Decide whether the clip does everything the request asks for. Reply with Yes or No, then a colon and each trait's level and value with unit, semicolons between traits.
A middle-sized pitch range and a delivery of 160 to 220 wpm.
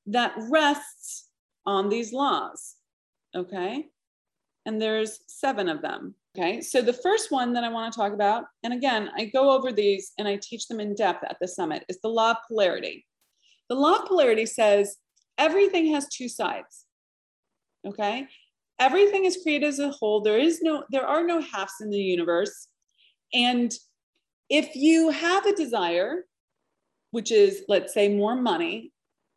No: wide, 6.7 semitones; average, 165 wpm